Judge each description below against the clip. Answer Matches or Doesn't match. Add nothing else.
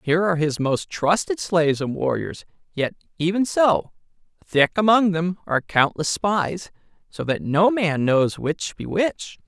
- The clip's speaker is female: Doesn't match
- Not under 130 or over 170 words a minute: Matches